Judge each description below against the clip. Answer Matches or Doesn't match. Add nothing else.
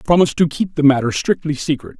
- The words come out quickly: Matches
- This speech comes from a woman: Doesn't match